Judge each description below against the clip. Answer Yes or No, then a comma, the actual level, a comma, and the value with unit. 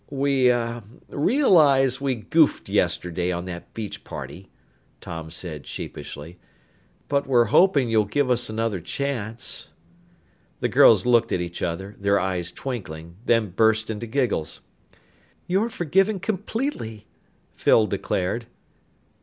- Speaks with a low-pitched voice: Yes, low, 115 Hz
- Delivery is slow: Yes, slow, 120 wpm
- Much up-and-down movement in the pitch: Yes, wide, 6.9 semitones